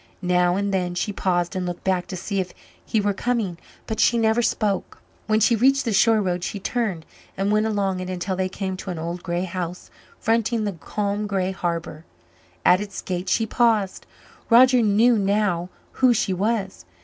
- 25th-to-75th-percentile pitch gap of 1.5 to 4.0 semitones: Yes, average, 3.3 semitones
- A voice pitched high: Yes, high, 195 Hz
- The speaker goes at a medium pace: Yes, average, 190 wpm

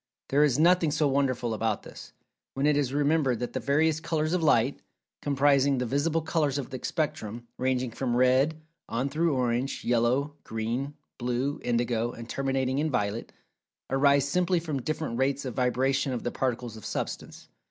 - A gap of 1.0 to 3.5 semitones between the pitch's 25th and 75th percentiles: Yes, average, 3.2 semitones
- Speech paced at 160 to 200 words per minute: Yes, average, 170 wpm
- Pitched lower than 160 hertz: Yes, low, 135 Hz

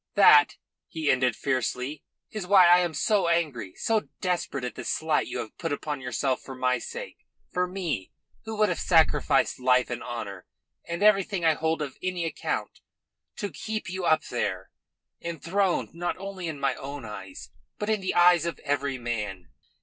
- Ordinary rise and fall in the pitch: No, wide, 6.0 semitones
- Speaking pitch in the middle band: Yes, medium, 160 Hz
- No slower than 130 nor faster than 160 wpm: No, average, 175 wpm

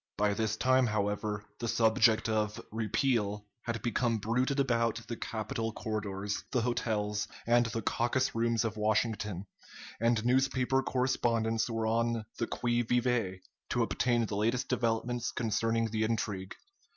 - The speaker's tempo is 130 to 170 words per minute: Yes, average, 140 wpm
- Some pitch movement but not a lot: No, narrow, 2.0 semitones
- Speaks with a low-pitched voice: Yes, low, 115 Hz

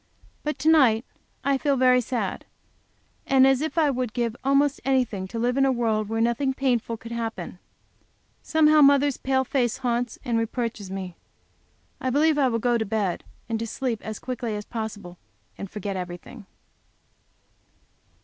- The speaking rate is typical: Yes, average, 170 wpm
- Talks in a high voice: Yes, high, 240 Hz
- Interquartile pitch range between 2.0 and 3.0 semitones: No, average, 3.4 semitones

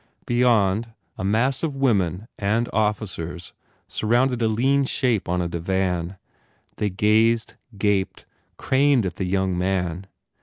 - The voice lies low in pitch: Yes, low, 105 Hz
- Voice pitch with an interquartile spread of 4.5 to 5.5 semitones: No, average, 4.1 semitones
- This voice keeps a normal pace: No, slow, 125 wpm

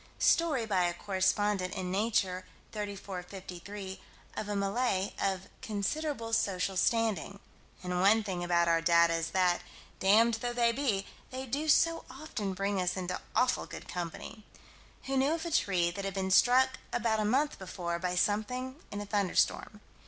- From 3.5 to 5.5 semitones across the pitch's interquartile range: Yes, average, 4.1 semitones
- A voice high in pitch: Yes, high, 200 Hz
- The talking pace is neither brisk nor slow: Yes, average, 165 wpm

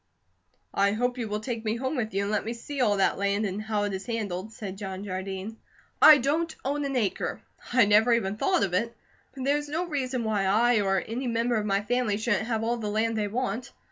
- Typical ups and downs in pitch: Yes, average, 3.4 semitones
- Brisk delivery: Yes, fast, 240 wpm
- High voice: Yes, high, 220 Hz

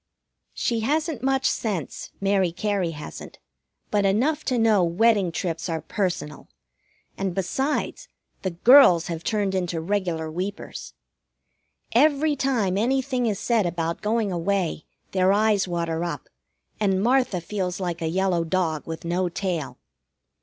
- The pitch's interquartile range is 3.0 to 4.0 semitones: No, average, 4.7 semitones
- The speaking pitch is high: Yes, high, 195 Hz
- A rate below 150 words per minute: Yes, slow, 135 wpm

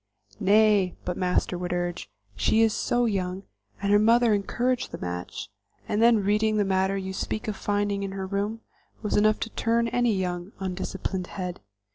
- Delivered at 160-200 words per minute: Yes, average, 170 wpm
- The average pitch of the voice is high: Yes, high, 200 Hz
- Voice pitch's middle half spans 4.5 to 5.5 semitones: No, average, 2.7 semitones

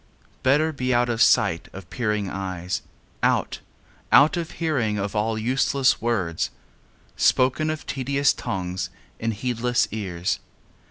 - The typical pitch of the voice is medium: No, low, 115 Hz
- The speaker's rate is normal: No, slow, 125 wpm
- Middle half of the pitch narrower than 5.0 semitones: No, average, 5.3 semitones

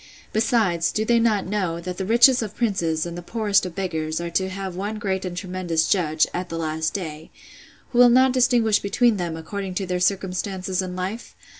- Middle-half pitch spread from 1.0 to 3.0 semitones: No, average, 3.7 semitones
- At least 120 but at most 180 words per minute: No, average, 200 wpm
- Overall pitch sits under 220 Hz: Yes, high, 190 Hz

